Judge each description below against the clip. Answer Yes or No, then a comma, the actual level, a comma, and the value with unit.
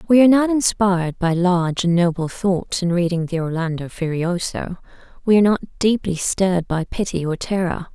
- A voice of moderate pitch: Yes, medium, 180 Hz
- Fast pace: No, average, 175 wpm